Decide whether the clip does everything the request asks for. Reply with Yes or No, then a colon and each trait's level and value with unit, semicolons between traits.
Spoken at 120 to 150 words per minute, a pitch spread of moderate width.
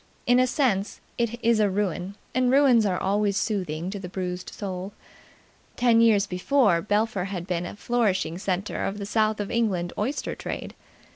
No: average, 170 wpm; average, 3.9 semitones